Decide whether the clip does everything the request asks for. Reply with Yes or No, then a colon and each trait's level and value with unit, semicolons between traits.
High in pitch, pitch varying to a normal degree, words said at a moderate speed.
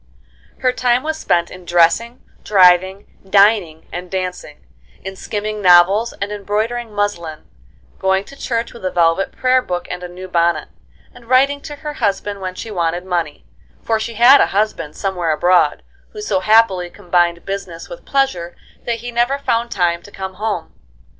Yes: high, 195 Hz; average, 4.7 semitones; average, 165 wpm